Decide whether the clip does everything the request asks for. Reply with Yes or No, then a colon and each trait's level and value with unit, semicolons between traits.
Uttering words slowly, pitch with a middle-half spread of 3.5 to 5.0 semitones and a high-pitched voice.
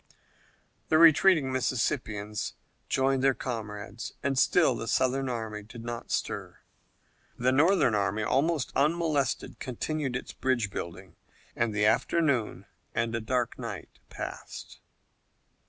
No: slow, 120 wpm; average, 4.1 semitones; low, 125 Hz